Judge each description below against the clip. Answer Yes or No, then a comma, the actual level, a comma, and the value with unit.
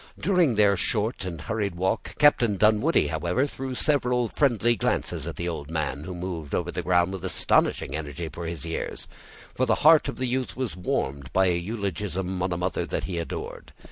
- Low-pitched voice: Yes, very low, 95 Hz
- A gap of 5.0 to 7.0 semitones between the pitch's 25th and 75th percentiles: Yes, wide, 5.6 semitones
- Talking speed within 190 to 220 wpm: Yes, average, 195 wpm